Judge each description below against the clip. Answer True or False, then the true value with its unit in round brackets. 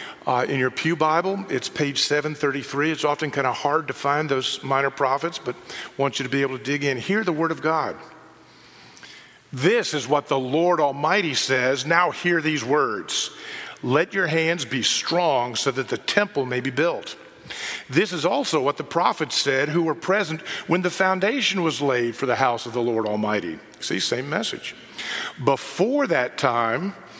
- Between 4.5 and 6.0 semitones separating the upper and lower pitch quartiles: False (3.8 semitones)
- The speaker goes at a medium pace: True (190 wpm)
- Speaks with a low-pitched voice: False (145 Hz)